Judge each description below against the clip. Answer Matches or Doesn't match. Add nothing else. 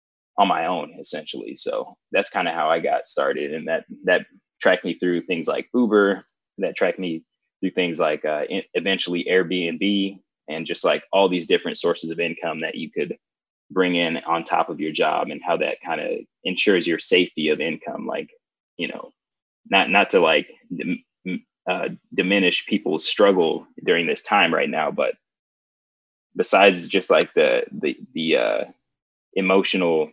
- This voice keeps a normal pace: Matches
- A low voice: Matches